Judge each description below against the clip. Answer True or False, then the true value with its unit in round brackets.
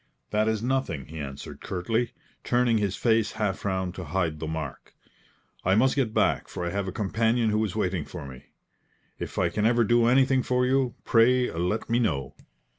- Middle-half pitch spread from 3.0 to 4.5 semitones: False (5.0 semitones)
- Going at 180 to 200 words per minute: True (190 wpm)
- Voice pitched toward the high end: False (110 Hz)